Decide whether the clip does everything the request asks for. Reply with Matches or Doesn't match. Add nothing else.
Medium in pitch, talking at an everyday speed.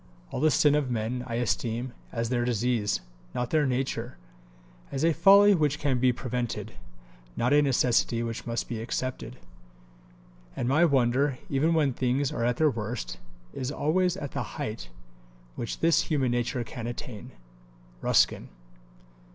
Doesn't match